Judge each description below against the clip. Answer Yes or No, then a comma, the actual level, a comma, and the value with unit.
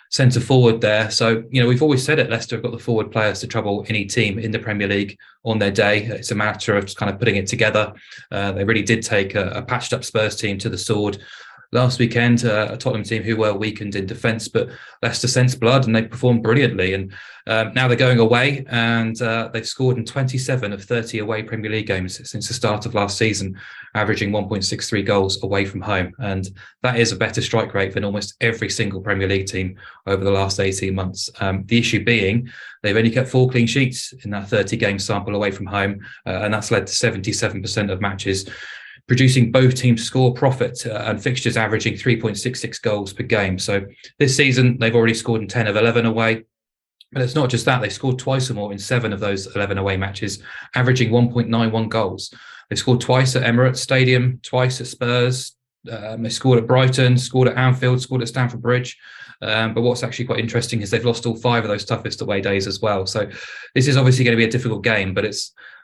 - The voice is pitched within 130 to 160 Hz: No, low, 115 Hz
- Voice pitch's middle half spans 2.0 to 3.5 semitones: Yes, average, 3.2 semitones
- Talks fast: Yes, fast, 220 wpm